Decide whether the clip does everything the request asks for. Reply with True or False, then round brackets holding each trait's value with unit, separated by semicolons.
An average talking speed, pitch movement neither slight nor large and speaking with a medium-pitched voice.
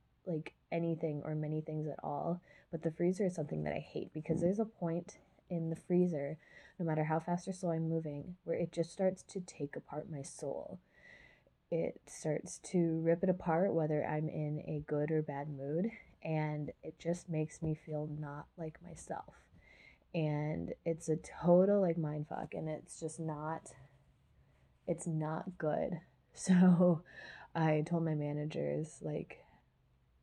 False (165 wpm; 2.3 semitones; 160 Hz)